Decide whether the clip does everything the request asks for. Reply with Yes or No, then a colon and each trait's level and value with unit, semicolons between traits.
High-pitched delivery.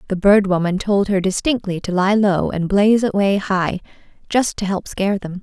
Yes: high, 195 Hz